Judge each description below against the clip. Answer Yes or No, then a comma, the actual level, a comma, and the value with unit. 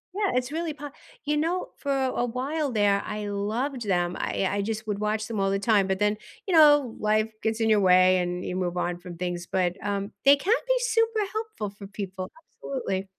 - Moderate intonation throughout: No, wide, 6.5 semitones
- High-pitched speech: Yes, high, 215 Hz